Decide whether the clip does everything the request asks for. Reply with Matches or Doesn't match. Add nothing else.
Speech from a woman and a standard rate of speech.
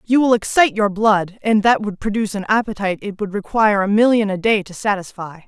Doesn't match